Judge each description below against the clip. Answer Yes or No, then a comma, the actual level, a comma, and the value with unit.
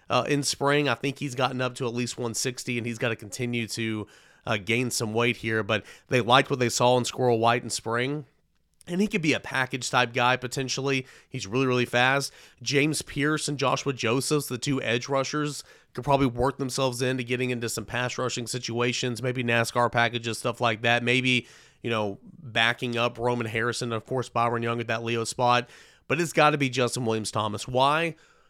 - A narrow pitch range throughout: Yes, narrow, 2.3 semitones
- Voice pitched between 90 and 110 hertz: No, low, 125 Hz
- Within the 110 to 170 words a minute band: No, fast, 205 wpm